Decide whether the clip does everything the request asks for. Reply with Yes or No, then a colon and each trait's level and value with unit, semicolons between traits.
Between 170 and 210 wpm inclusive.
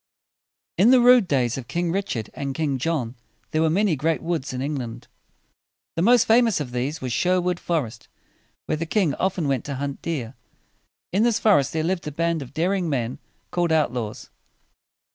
Yes: average, 190 wpm